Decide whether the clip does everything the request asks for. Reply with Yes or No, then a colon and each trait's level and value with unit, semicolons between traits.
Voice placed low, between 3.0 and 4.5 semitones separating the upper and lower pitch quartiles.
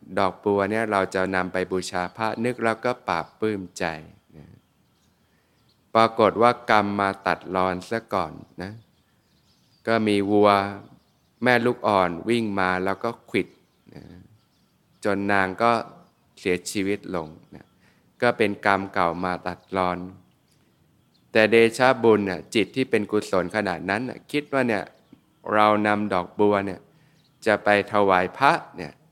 Yes: low, 100 Hz; average, 3.7 semitones